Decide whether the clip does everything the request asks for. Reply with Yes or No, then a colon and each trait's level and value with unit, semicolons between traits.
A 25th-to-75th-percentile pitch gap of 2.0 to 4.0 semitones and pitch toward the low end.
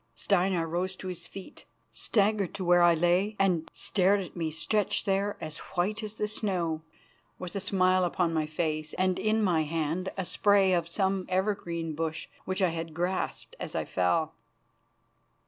No: average, 2.9 semitones; medium, 180 Hz